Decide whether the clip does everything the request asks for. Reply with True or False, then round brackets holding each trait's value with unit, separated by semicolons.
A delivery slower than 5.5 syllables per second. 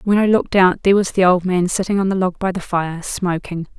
False (5.9 syllables/s)